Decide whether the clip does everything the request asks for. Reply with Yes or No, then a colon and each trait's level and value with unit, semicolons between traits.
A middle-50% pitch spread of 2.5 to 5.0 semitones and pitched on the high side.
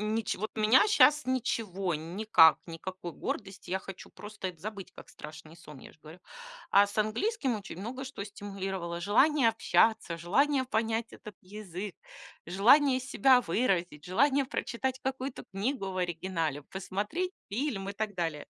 No: wide, 5.6 semitones; high, 205 Hz